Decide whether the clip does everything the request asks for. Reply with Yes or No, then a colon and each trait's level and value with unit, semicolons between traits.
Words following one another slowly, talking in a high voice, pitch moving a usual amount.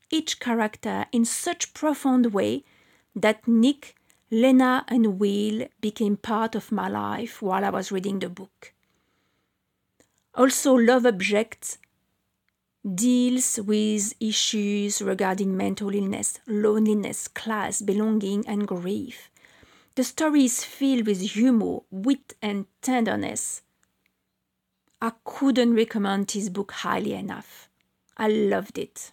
Yes: slow, 115 wpm; high, 220 Hz; average, 3.4 semitones